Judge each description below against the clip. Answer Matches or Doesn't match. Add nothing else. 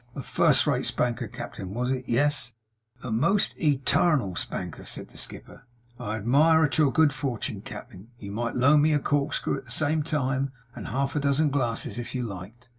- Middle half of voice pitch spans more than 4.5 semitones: Doesn't match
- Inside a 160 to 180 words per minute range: Doesn't match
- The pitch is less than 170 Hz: Matches